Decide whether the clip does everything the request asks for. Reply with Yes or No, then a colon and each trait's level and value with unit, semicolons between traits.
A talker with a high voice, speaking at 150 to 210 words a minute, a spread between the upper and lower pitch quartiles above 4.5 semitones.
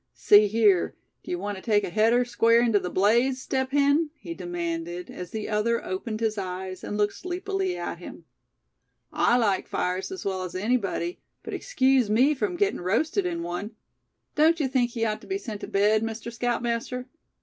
Yes: high, 225 Hz; average, 185 wpm; average, 5.0 semitones